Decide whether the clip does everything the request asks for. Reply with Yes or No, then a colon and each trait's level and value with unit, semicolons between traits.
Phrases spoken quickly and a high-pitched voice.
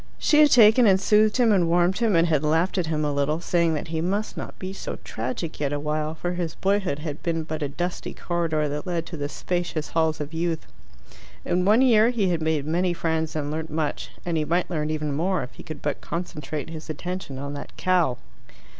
No: fast, 225 wpm; medium, 165 Hz